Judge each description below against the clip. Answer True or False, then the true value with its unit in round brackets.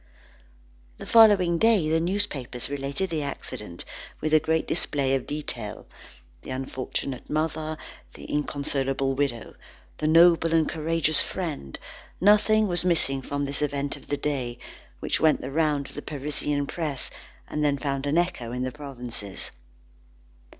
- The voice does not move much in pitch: False (3.2 semitones)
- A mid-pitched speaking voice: True (145 Hz)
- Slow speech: False (145 wpm)